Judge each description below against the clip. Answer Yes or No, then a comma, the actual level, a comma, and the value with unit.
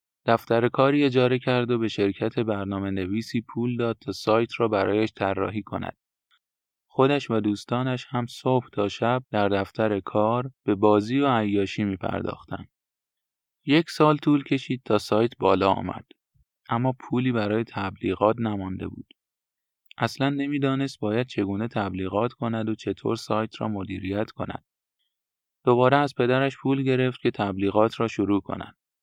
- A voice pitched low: Yes, low, 115 Hz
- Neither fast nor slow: Yes, average, 145 wpm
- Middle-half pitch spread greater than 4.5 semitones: No, average, 3.9 semitones